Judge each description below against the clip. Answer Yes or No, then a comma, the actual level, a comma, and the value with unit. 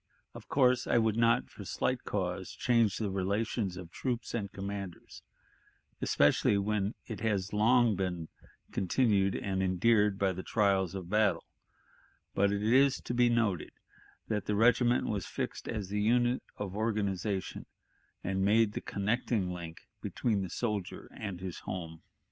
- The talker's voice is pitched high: No, low, 105 Hz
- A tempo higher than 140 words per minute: Yes, average, 150 wpm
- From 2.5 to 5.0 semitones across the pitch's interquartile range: Yes, average, 3.2 semitones